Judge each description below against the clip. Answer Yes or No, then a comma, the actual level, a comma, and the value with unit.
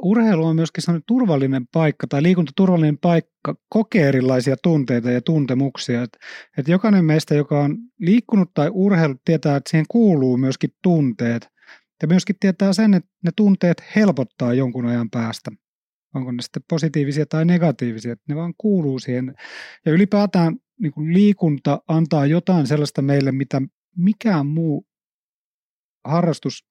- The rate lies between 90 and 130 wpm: No, average, 145 wpm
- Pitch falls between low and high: Yes, medium, 160 Hz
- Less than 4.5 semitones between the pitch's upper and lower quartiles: No, average, 4.9 semitones